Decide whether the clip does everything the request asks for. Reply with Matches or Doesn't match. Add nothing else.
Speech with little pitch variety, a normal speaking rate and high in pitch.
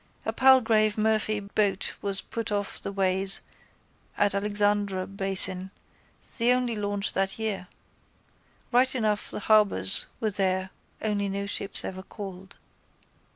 Doesn't match